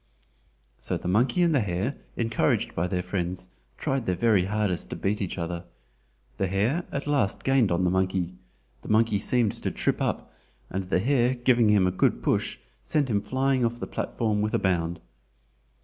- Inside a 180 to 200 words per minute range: Yes, average, 185 wpm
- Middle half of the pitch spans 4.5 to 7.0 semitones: Yes, average, 4.9 semitones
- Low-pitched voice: Yes, low, 105 Hz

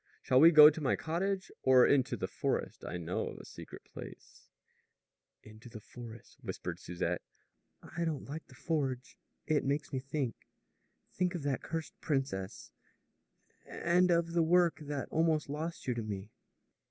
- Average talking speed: Yes, average, 165 wpm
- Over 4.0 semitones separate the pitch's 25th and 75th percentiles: Yes, average, 4.7 semitones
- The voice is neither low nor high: Yes, medium, 145 Hz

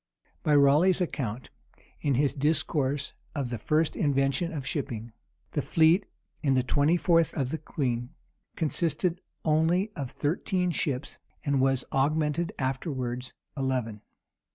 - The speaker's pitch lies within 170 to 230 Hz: No, medium, 145 Hz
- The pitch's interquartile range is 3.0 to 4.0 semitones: Yes, average, 3.5 semitones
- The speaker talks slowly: Yes, slow, 130 wpm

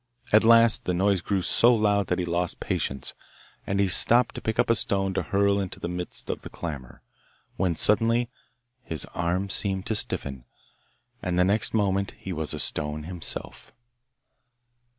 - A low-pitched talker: Yes, very low, 95 Hz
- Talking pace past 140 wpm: Yes, average, 170 wpm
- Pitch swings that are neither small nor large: Yes, average, 3.1 semitones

